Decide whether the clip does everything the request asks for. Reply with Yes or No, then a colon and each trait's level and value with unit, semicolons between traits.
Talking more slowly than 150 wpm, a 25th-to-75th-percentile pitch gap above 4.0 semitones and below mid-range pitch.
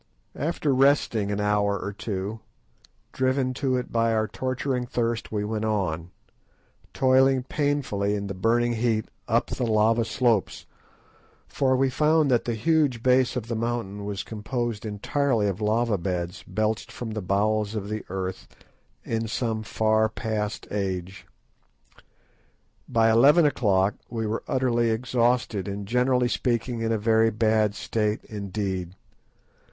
No: average, 140 wpm; average, 3.2 semitones; low, 110 Hz